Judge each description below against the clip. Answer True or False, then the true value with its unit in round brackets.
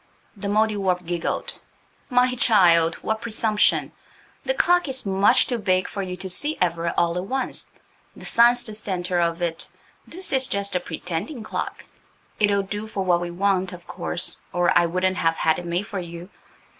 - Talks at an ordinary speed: True (175 wpm)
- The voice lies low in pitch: False (190 Hz)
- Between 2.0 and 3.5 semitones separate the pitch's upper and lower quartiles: False (3.9 semitones)